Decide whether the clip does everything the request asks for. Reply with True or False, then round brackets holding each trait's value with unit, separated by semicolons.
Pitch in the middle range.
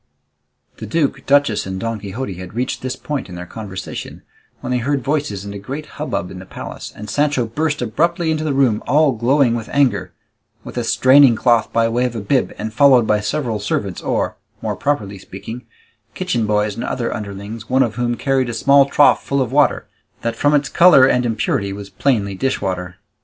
False (120 Hz)